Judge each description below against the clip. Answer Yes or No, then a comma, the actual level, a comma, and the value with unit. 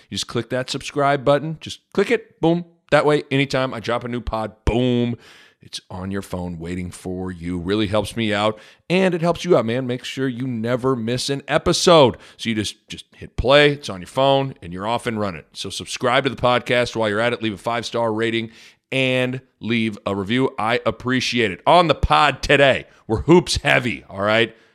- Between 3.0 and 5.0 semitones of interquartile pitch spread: Yes, average, 4.0 semitones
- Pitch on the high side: No, low, 120 Hz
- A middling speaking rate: No, fast, 215 wpm